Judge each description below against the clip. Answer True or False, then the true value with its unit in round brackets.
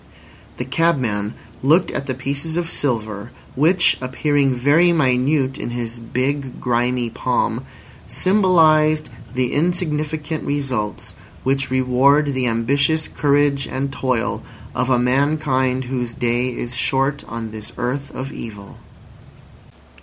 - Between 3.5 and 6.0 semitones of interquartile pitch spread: False (3.1 semitones)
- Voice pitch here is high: False (135 Hz)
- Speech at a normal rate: False (120 wpm)